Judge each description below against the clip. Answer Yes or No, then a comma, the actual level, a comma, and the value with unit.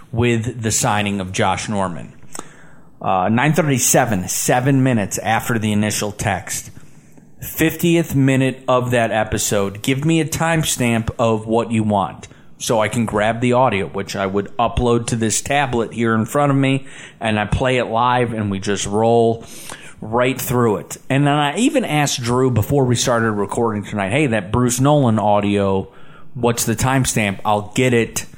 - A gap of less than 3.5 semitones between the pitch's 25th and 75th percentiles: No, average, 3.9 semitones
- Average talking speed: Yes, average, 165 wpm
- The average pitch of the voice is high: No, low, 120 Hz